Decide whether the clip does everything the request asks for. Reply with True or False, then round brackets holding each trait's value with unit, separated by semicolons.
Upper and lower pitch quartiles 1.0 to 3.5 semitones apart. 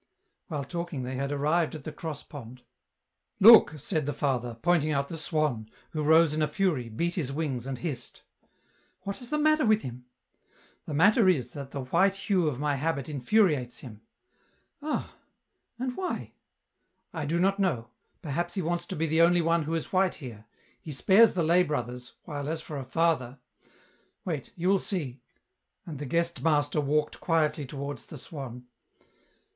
False (4.1 semitones)